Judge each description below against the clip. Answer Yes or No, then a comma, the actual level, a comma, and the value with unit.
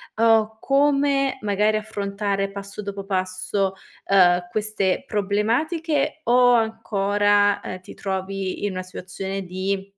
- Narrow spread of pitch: Yes, narrow, 2.3 semitones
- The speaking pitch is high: Yes, high, 200 Hz